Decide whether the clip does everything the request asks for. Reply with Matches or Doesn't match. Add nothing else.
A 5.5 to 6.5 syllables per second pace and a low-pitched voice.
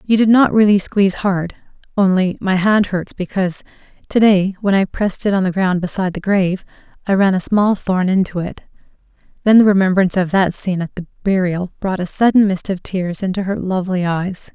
Doesn't match